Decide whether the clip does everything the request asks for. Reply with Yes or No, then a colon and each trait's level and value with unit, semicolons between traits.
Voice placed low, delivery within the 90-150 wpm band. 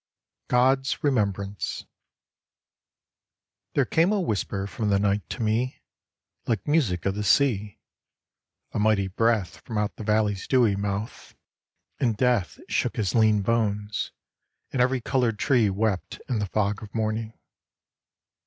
Yes: low, 110 Hz; slow, 135 wpm